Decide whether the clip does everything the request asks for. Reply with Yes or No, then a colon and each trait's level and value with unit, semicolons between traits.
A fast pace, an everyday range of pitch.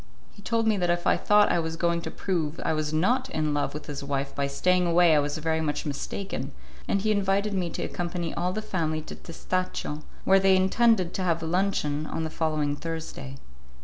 Yes: fast, 215 wpm; average, 3.6 semitones